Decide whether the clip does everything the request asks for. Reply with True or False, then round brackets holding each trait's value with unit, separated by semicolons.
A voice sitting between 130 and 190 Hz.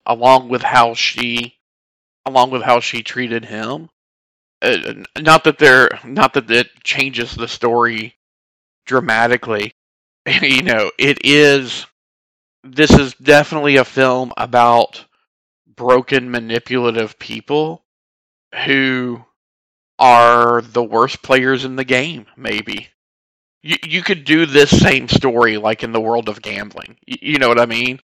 False (120 Hz)